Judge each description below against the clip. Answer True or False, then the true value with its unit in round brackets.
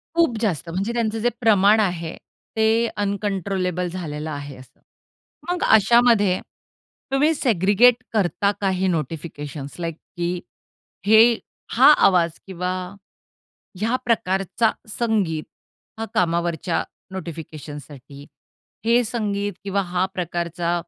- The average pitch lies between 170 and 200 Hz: True (190 Hz)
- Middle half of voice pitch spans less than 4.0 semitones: False (4.7 semitones)